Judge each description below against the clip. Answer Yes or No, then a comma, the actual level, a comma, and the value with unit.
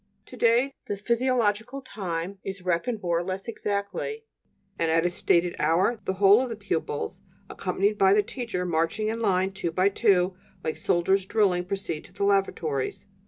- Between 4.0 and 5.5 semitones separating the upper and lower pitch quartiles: No, average, 3.3 semitones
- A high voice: Yes, high, 195 Hz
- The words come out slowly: No, average, 170 wpm